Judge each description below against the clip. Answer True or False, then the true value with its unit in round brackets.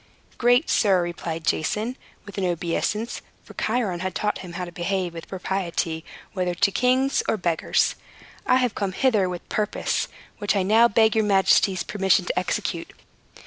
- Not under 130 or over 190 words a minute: True (170 wpm)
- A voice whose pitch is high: True (195 Hz)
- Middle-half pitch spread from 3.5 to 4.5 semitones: True (3.8 semitones)